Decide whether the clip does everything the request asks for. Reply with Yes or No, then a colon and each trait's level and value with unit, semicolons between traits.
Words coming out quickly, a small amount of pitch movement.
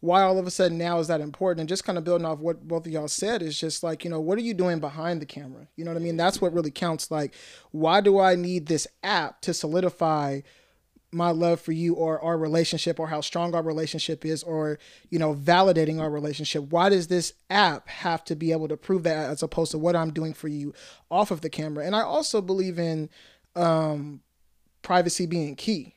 Yes: fast, 235 wpm; narrow, 2.0 semitones